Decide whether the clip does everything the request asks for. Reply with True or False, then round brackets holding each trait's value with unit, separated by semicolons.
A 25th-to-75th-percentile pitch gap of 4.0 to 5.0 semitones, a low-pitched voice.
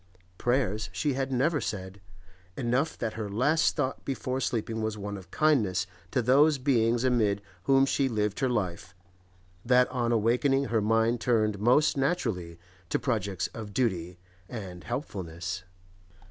True (4.5 semitones; 115 Hz)